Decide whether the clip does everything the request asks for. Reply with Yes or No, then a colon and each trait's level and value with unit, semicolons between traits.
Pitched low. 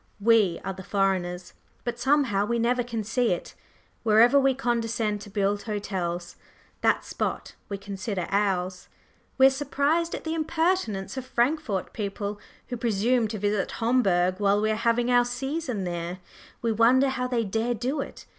No: high, 225 Hz